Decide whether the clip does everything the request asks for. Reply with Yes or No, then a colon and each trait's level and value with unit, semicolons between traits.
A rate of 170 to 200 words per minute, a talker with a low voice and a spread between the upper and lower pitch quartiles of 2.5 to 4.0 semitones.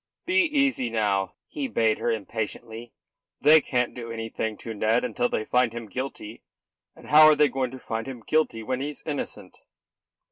No: average, 175 wpm; low, 120 Hz; average, 4.6 semitones